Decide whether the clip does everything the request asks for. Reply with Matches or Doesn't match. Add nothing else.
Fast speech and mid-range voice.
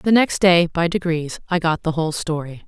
Matches